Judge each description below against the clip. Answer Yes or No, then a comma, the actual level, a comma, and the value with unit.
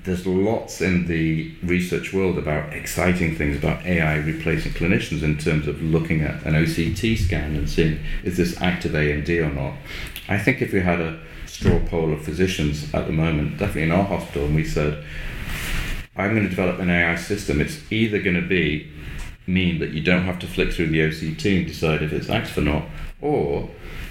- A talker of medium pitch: No, very low, 80 Hz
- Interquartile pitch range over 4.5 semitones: No, average, 2.9 semitones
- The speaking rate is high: No, average, 195 wpm